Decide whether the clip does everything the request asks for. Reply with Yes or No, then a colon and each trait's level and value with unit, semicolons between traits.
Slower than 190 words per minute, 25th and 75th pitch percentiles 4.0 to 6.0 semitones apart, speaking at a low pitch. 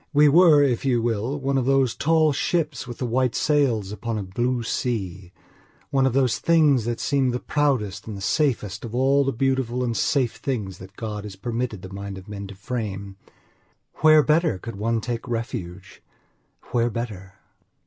Yes: average, 180 wpm; average, 4.6 semitones; low, 120 Hz